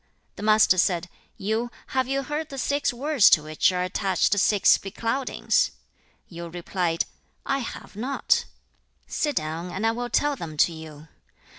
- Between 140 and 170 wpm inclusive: Yes, average, 160 wpm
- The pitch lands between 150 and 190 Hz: No, high, 210 Hz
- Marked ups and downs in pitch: Yes, wide, 7.4 semitones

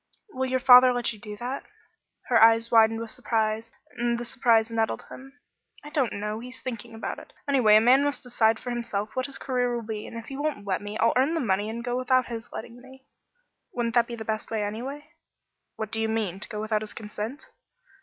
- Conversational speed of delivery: No, fast, 225 wpm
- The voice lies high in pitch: Yes, high, 230 Hz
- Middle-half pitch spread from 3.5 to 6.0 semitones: No, narrow, 2.5 semitones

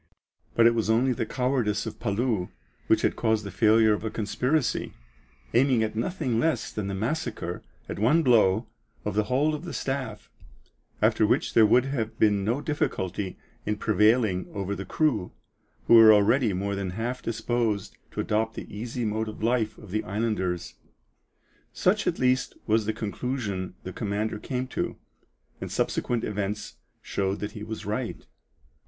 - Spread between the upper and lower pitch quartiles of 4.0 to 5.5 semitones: No, average, 3.2 semitones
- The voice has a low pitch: Yes, low, 110 Hz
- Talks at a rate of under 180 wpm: Yes, average, 165 wpm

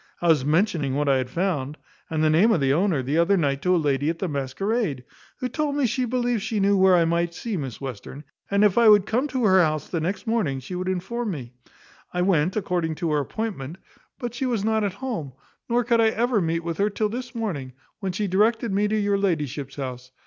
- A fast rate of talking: Yes, fast, 235 wpm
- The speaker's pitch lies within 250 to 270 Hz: No, medium, 185 Hz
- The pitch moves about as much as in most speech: No, wide, 6.5 semitones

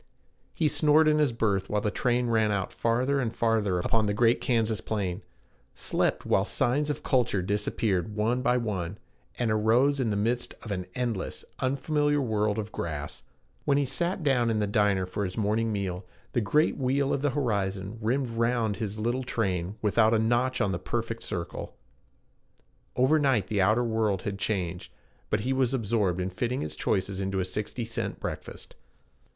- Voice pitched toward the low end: Yes, low, 110 Hz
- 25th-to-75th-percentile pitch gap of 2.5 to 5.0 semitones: Yes, average, 3.7 semitones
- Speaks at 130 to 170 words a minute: No, average, 180 wpm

